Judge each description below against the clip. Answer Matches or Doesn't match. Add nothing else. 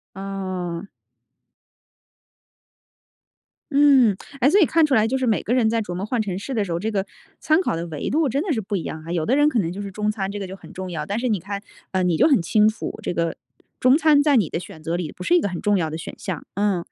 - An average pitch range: Doesn't match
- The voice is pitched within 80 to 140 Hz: Doesn't match